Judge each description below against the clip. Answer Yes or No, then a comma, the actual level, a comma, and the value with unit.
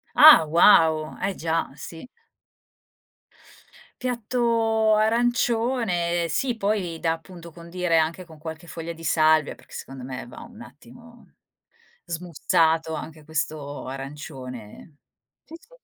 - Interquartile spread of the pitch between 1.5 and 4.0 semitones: No, wide, 6.0 semitones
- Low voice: No, medium, 170 Hz